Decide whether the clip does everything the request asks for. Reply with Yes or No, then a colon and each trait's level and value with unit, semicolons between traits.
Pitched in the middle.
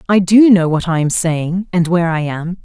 Yes: medium, 175 Hz